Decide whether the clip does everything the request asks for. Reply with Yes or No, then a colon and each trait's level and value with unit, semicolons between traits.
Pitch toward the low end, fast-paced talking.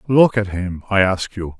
Yes: low, 100 Hz; fast, 225 wpm